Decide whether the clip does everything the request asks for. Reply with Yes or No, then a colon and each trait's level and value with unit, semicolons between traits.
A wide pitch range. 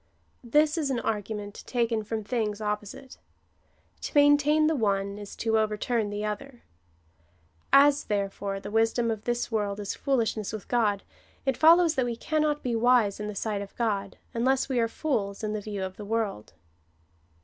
No: average, 3.8 semitones